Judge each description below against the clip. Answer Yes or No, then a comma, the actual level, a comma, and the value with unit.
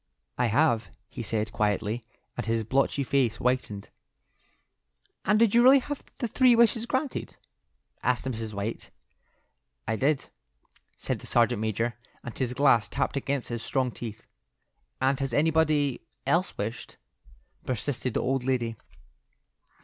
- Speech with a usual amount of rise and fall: Yes, average, 4.4 semitones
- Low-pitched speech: Yes, low, 125 Hz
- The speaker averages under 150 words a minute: Yes, slow, 135 wpm